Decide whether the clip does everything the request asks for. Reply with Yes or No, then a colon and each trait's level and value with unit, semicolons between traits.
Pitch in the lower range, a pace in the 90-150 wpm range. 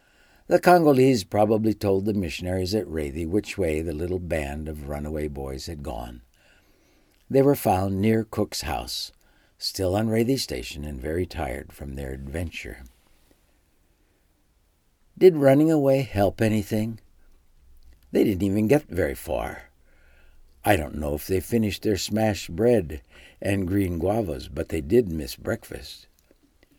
Yes: very low, 90 Hz; average, 140 wpm